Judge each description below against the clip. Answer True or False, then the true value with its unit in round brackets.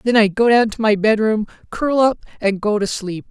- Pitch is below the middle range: False (215 Hz)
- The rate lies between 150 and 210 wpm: False (235 wpm)